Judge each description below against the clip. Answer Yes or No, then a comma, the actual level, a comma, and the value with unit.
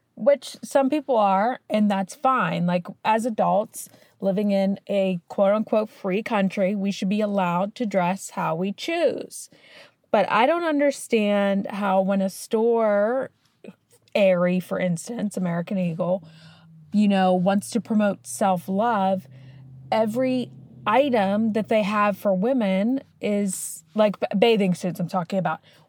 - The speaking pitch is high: Yes, high, 200 Hz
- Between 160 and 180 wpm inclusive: No, average, 140 wpm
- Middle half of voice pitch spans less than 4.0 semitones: Yes, average, 3.1 semitones